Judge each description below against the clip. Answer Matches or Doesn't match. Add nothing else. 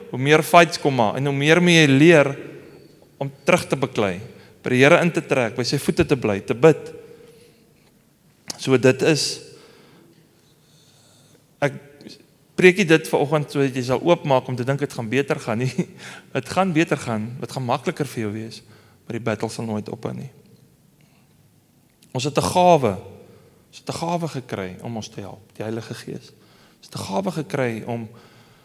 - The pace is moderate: Matches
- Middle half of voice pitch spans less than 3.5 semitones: Doesn't match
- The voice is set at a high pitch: Doesn't match